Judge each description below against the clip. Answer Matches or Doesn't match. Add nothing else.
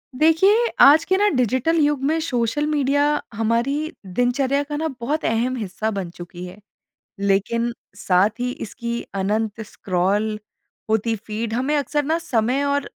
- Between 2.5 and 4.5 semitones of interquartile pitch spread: Doesn't match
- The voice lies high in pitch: Matches